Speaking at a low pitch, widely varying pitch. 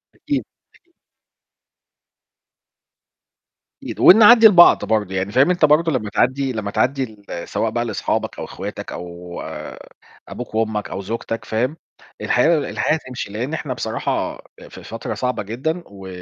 Yes: low, 125 Hz; wide, 6.4 semitones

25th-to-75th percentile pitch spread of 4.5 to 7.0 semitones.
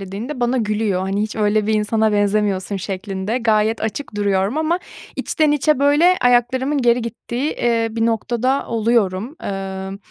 No: average, 3.4 semitones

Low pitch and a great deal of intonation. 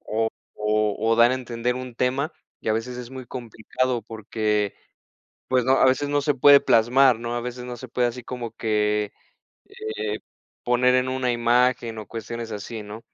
No: low, 120 Hz; narrow, 2.4 semitones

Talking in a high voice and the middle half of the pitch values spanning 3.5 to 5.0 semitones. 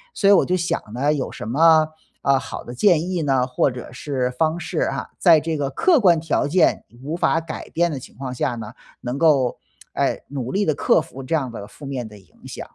No: medium, 145 Hz; average, 4.6 semitones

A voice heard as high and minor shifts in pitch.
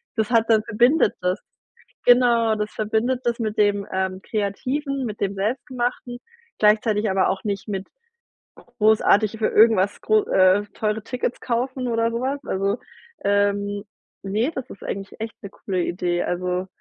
No: high, 215 Hz; average, 3.1 semitones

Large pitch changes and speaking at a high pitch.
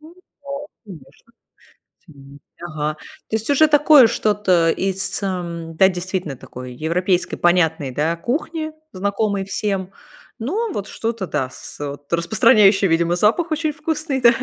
Yes: wide, 7.0 semitones; high, 195 Hz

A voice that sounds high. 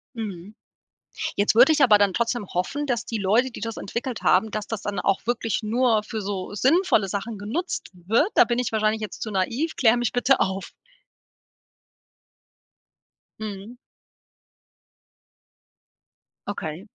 Yes: high, 220 Hz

